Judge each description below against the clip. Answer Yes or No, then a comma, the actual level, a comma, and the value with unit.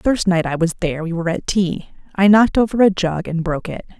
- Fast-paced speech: Yes, fast, 270 wpm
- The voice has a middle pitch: Yes, medium, 180 Hz